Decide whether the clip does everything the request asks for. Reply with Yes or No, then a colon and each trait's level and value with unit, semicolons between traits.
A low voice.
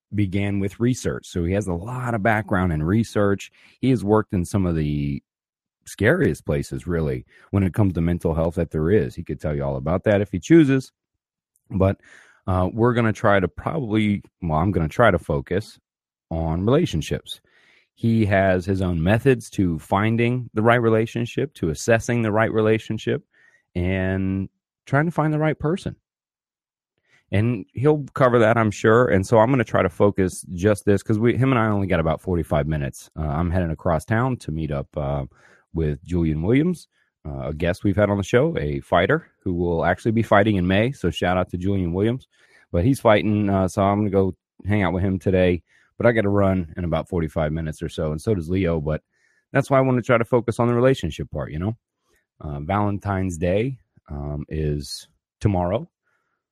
Yes: low, 100 Hz